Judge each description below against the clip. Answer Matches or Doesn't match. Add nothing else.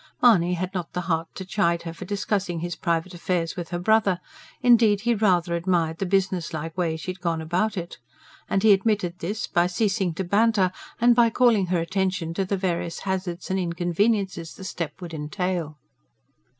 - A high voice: Doesn't match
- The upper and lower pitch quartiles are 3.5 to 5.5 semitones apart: Doesn't match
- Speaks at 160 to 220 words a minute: Matches